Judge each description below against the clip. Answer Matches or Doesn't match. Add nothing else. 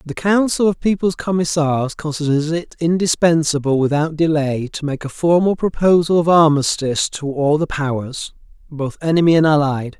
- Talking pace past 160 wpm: Doesn't match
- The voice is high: Doesn't match